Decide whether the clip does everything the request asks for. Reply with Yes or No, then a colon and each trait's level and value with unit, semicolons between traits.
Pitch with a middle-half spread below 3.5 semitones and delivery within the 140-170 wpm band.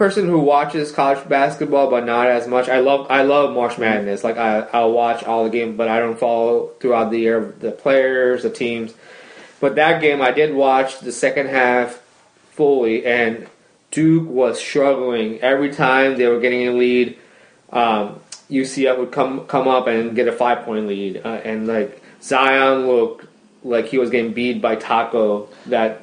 No: average, 2.9 semitones; average, 180 wpm